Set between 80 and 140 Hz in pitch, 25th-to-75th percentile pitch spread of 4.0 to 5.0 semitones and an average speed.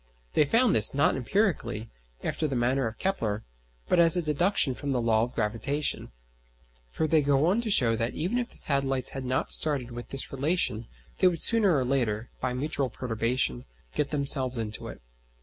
Yes: low, 135 Hz; average, 4.7 semitones; average, 185 wpm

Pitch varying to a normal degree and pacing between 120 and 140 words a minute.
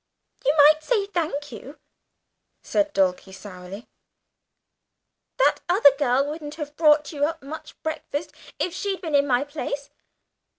No: narrow, 2.3 semitones; slow, 135 wpm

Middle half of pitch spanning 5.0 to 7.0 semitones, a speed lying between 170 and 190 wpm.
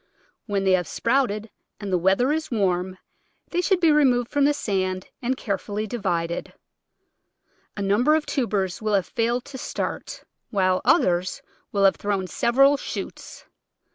No: wide, 5.5 semitones; average, 160 wpm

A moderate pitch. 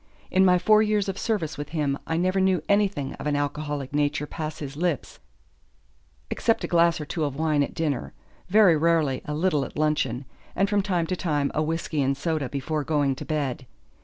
Yes: medium, 155 Hz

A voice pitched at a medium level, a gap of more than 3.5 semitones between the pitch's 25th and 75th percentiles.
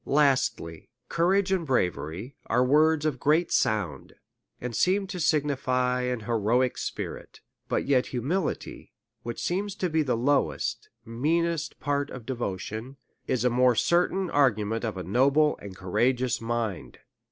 No: low, 130 Hz; average, 5.1 semitones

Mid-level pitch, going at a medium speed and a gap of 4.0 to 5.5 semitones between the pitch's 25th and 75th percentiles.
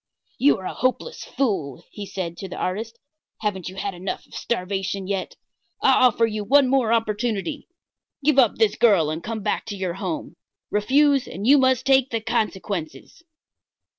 No: high, 215 Hz; average, 170 wpm; average, 5.0 semitones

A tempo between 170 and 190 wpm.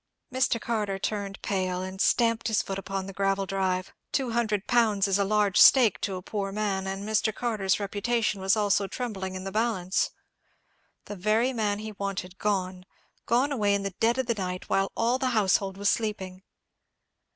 Yes: average, 180 wpm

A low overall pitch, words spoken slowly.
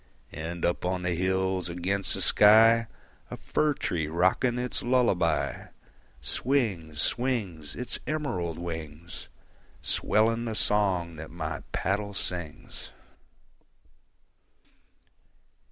Yes: very low, 95 Hz; slow, 100 wpm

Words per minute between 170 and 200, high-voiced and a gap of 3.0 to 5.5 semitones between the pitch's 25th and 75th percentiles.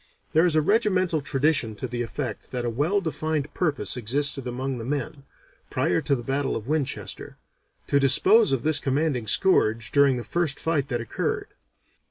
No: average, 175 wpm; medium, 140 Hz; average, 4.2 semitones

